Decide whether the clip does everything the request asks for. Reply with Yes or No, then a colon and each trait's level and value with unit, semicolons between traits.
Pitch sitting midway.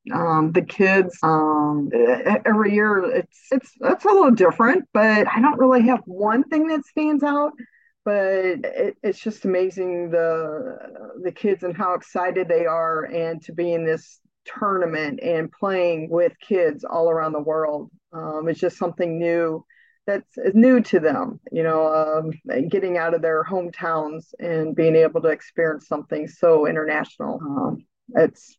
Yes: medium, 180 Hz